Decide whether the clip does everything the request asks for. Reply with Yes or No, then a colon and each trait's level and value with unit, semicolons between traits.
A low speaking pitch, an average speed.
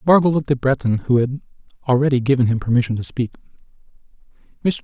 Yes: low, 130 Hz; average, 160 wpm